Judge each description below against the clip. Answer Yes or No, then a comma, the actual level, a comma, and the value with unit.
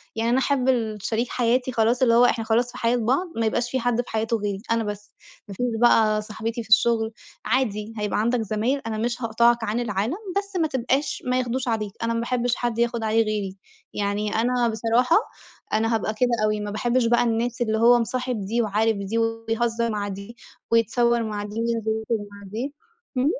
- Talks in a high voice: Yes, high, 230 Hz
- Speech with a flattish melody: Yes, narrow, 2.0 semitones